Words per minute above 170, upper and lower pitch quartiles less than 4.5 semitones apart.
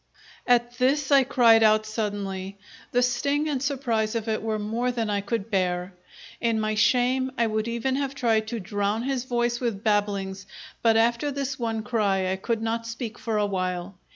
Yes: average, 185 wpm; average, 3.0 semitones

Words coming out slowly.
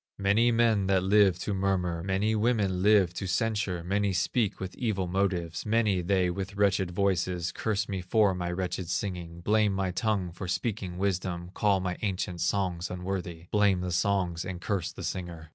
No: average, 175 wpm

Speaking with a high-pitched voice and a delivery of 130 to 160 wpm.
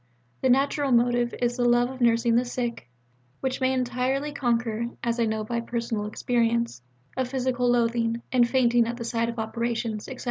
No: high, 240 Hz; average, 180 wpm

